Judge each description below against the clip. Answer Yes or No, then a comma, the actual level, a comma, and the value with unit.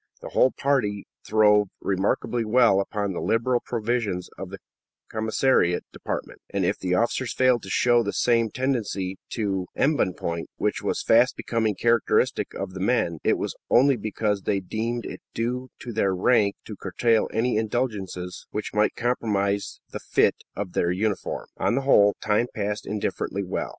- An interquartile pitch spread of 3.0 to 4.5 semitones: Yes, average, 3.3 semitones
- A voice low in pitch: Yes, low, 110 Hz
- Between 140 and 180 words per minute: Yes, average, 160 wpm